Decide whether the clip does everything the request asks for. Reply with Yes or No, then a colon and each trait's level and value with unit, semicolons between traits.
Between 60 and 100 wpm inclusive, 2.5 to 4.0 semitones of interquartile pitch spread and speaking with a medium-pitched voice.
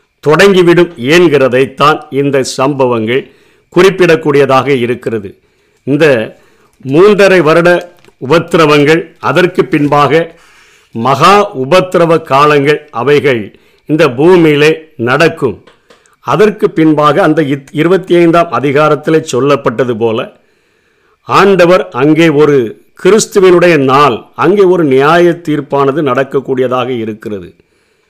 No: average, 80 wpm; average, 4.4 semitones; medium, 155 Hz